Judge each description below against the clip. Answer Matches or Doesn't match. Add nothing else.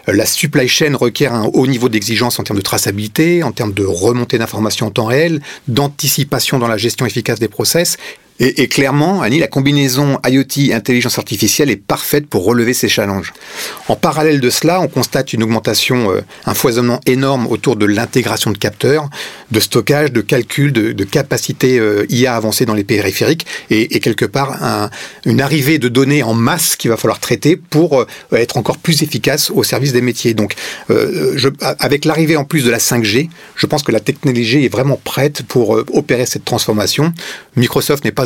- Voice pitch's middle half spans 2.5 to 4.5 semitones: Matches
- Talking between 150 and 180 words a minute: Doesn't match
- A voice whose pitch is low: Matches